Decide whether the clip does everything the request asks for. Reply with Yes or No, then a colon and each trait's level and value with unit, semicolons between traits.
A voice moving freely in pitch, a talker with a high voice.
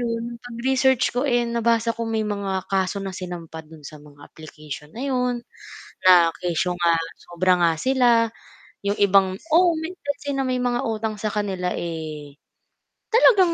Yes: wide, 5.8 semitones; high, 215 Hz